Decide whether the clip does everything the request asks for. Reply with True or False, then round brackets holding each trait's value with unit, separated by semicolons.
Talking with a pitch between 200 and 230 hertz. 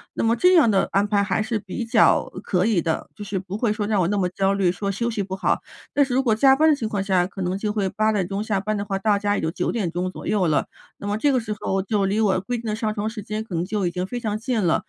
True (205 Hz)